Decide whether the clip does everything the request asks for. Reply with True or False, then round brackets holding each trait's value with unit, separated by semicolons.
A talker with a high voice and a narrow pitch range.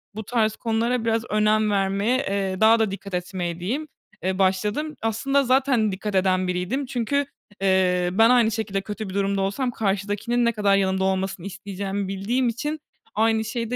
False (210 Hz; 3.2 semitones)